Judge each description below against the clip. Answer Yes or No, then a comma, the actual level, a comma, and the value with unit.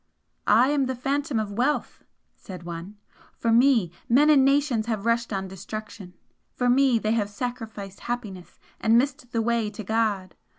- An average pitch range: Yes, average, 3.6 semitones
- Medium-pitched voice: No, high, 230 Hz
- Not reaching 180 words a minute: Yes, average, 165 wpm